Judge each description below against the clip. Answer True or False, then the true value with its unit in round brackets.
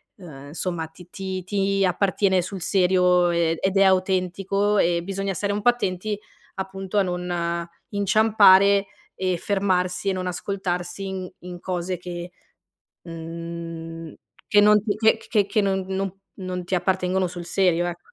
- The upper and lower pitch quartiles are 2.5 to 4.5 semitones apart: False (1.9 semitones)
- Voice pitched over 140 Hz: True (185 Hz)